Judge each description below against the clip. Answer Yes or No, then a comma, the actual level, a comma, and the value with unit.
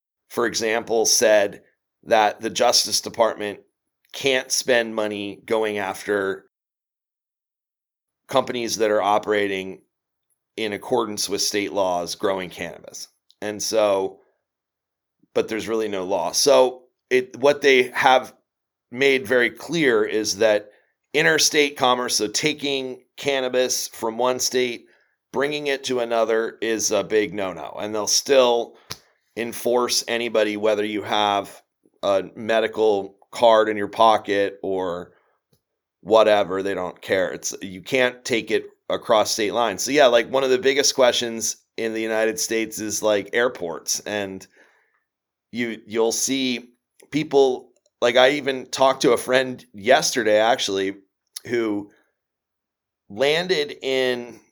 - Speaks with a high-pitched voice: No, low, 115 Hz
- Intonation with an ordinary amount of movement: Yes, average, 3.5 semitones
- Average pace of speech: No, slow, 125 wpm